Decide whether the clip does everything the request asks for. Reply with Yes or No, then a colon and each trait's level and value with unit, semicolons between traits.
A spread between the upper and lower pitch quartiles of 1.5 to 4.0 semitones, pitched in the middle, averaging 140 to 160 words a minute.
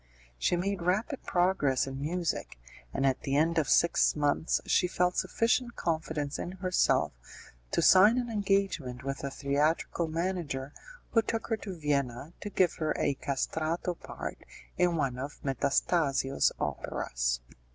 No: average, 4.8 semitones; medium, 160 Hz; average, 145 wpm